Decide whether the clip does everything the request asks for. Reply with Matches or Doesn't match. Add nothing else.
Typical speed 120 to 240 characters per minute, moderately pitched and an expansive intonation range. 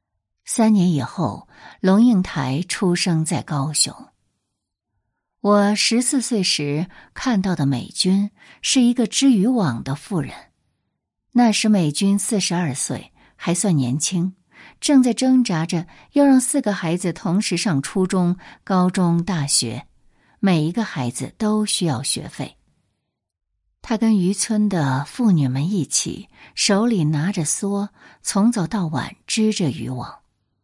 Matches